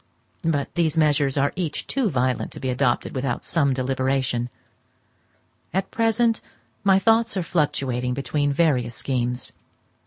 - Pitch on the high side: No, medium, 140 Hz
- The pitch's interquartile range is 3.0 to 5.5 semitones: Yes, average, 5.0 semitones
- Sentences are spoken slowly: Yes, slow, 130 wpm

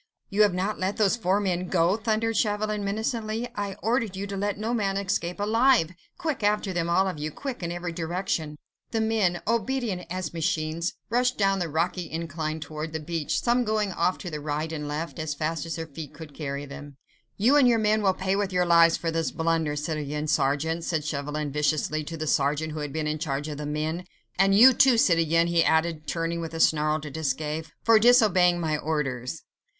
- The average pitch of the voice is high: No, medium, 170 Hz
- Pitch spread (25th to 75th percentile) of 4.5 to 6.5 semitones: Yes, average, 4.8 semitones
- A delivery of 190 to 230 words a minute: Yes, fast, 205 wpm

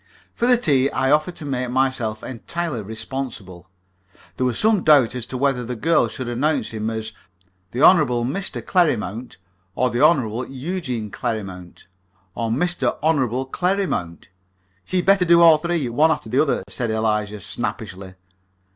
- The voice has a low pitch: Yes, low, 130 Hz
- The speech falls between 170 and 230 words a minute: No, average, 155 wpm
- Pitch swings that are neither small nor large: No, wide, 6.0 semitones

